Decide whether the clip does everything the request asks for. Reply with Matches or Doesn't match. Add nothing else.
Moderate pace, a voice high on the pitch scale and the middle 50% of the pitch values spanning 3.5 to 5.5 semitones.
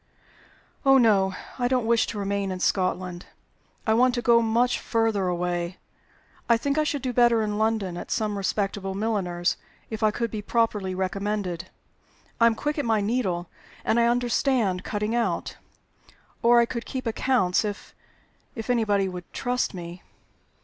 Matches